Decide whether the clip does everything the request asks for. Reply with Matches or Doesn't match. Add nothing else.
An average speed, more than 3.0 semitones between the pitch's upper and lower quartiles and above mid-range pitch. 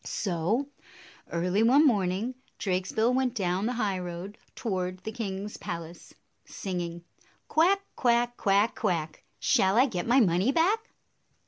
Doesn't match